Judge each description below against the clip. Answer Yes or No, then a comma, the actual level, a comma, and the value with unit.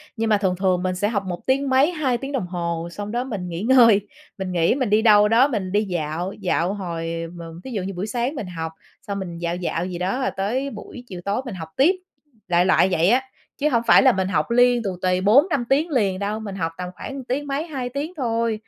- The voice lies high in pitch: Yes, high, 205 Hz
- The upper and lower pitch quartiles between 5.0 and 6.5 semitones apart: Yes, wide, 5.6 semitones